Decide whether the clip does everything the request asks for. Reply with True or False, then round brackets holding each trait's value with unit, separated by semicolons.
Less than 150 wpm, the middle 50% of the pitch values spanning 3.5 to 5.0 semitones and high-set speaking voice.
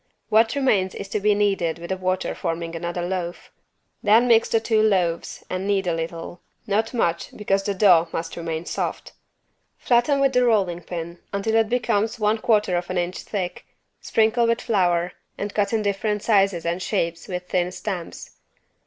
False (175 wpm; 3.8 semitones; 195 Hz)